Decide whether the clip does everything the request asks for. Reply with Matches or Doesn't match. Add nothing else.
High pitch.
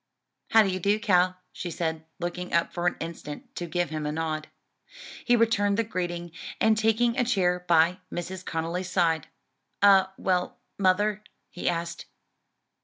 Doesn't match